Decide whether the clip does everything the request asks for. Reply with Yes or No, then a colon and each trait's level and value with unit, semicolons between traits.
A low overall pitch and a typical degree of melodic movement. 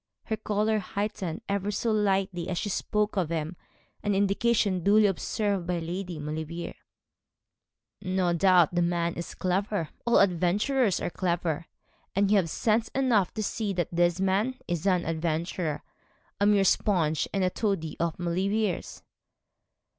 No: high, 190 Hz; average, 3.3 semitones